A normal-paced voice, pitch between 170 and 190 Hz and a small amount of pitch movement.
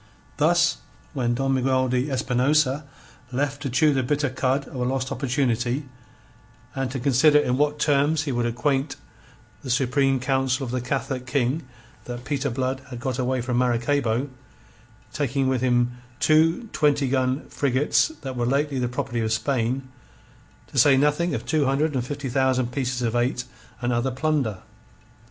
No: average, 165 wpm; low, 130 Hz; narrow, 2.3 semitones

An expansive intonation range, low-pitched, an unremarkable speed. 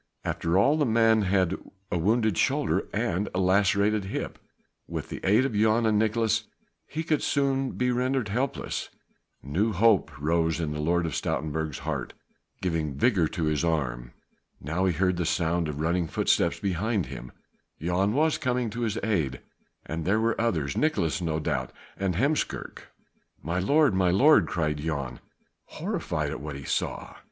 Yes: wide, 6.0 semitones; very low, 95 Hz; average, 165 wpm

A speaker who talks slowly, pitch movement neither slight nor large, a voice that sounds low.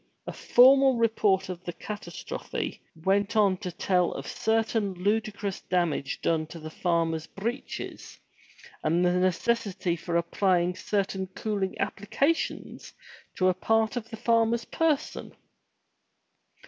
No: slow, 125 wpm; average, 4.0 semitones; high, 195 Hz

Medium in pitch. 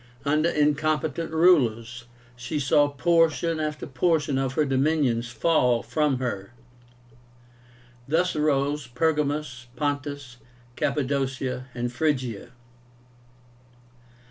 Yes: medium, 145 Hz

